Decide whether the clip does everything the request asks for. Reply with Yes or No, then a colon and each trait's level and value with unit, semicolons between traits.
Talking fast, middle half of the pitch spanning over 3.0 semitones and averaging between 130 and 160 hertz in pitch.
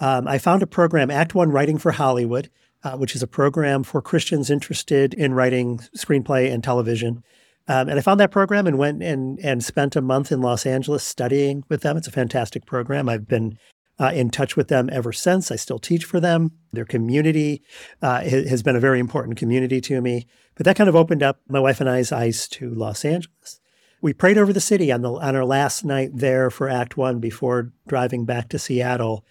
Yes: fast, 215 wpm; average, 3.4 semitones; low, 135 Hz